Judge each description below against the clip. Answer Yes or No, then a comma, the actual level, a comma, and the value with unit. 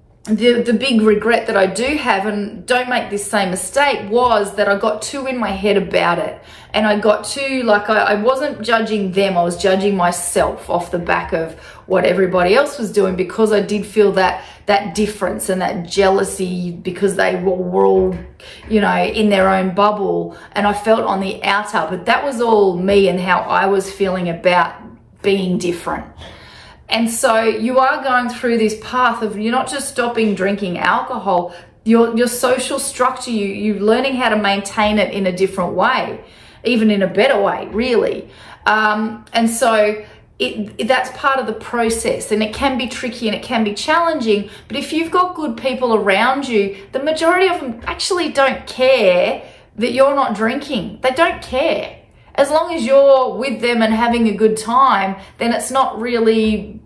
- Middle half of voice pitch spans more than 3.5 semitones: Yes, average, 4.1 semitones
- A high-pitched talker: Yes, high, 215 Hz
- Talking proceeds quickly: No, average, 190 wpm